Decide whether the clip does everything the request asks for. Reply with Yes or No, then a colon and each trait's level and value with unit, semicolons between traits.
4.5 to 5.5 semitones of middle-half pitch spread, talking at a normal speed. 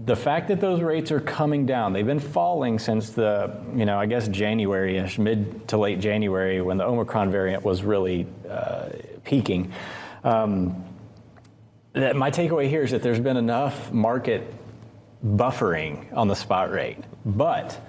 No: average, 3.3 semitones; average, 160 wpm